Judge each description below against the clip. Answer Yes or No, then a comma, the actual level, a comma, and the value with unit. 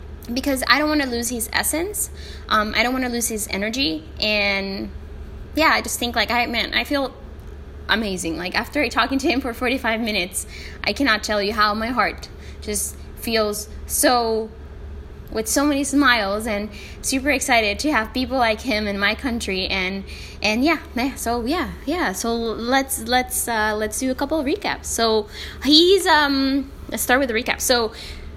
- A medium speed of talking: Yes, average, 180 wpm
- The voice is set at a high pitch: Yes, high, 235 Hz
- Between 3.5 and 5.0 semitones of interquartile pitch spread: Yes, average, 4.2 semitones